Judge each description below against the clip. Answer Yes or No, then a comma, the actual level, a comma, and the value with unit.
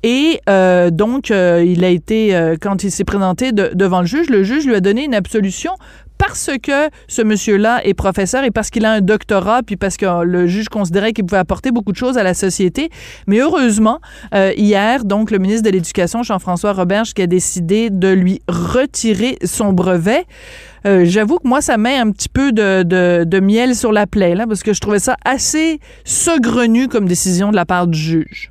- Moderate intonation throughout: Yes, average, 4.0 semitones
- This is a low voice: No, high, 205 Hz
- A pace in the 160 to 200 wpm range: No, average, 210 wpm